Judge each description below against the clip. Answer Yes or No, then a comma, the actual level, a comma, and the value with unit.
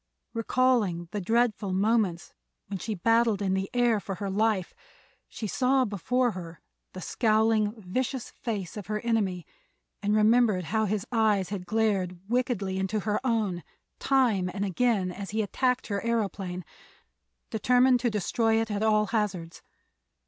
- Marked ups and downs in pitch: No, average, 3.2 semitones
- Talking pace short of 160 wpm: Yes, average, 150 wpm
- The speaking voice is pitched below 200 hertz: No, high, 210 Hz